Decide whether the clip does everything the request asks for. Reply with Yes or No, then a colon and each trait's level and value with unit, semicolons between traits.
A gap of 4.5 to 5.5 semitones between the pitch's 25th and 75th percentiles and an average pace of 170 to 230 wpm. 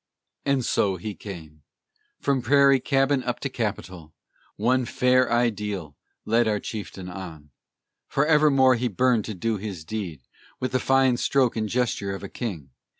No: average, 4.9 semitones; average, 150 wpm